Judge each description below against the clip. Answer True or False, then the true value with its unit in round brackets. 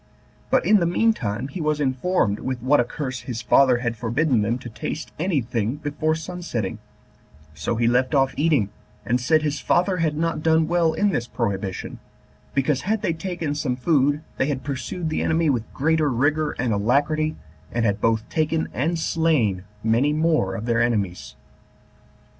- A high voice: False (140 Hz)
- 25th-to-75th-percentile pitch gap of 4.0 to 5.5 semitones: True (5.1 semitones)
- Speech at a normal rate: True (180 wpm)